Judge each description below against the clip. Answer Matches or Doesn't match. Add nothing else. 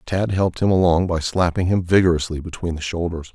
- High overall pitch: Doesn't match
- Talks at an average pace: Matches